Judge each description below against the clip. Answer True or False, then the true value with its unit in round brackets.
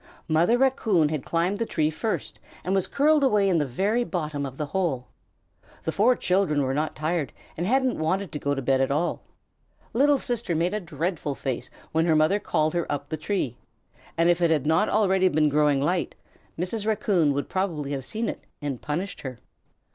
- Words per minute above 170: True (200 wpm)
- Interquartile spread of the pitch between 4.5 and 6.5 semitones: True (5.1 semitones)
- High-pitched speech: False (165 Hz)